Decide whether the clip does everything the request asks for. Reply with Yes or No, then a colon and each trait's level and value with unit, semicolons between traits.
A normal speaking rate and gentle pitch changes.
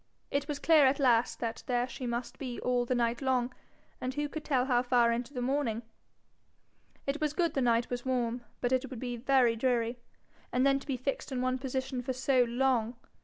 No: fast, 215 wpm; narrow, 1.9 semitones